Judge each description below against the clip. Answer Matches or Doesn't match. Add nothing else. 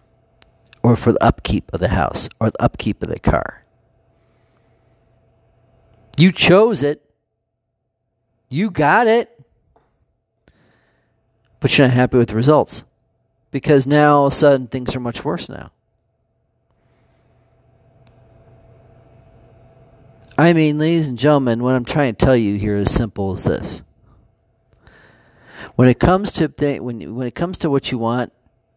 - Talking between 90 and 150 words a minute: Matches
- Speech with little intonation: Doesn't match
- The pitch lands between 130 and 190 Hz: Doesn't match